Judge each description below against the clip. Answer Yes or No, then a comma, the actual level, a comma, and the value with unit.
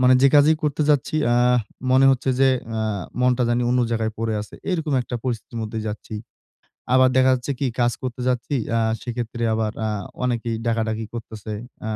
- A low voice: Yes, low, 120 Hz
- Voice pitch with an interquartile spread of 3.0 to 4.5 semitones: No, narrow, 2.5 semitones